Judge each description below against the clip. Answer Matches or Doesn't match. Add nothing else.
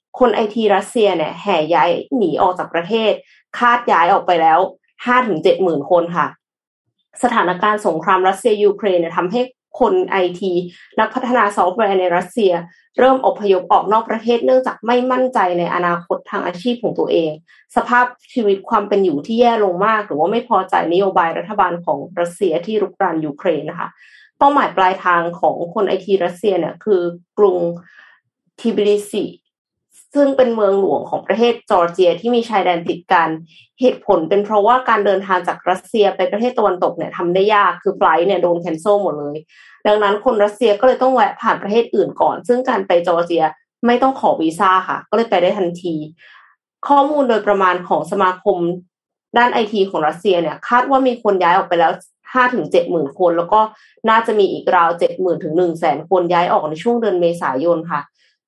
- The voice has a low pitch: Doesn't match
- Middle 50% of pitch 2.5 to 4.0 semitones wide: Doesn't match